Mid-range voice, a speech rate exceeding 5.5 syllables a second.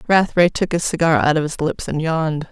Yes: medium, 160 Hz; 5.9 syllables/s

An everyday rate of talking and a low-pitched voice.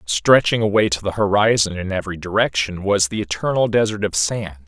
Yes: average, 180 wpm; low, 100 Hz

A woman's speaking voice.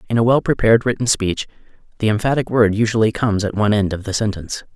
No: male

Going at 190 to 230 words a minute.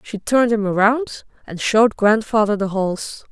No: average, 165 wpm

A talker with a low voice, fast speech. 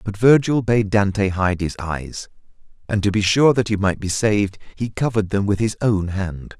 Yes: low, 100 Hz; fast, 210 wpm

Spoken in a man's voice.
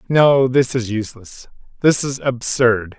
Yes: male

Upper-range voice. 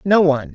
No: medium, 165 Hz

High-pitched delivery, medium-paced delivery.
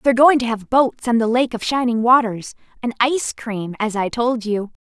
No: high, 235 Hz; fast, 210 wpm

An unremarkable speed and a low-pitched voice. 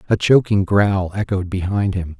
Yes: average, 165 wpm; low, 100 Hz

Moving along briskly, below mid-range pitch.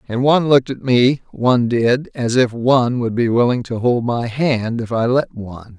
Yes: fast, 220 wpm; low, 120 Hz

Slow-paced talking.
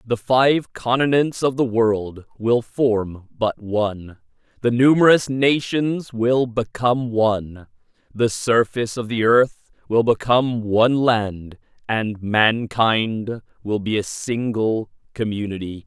Yes: slow, 120 wpm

